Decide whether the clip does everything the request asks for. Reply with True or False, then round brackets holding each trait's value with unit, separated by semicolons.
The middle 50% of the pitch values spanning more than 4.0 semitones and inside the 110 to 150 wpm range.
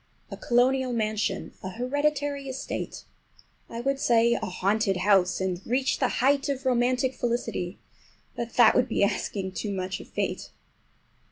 True (4.7 semitones; 145 wpm)